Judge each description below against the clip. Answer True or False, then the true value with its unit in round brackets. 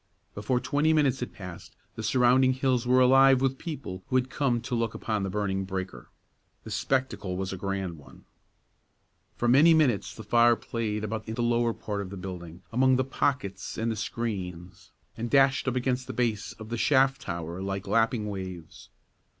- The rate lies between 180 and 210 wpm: True (185 wpm)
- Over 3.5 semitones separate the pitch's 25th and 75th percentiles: True (4.9 semitones)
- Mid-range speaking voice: False (115 Hz)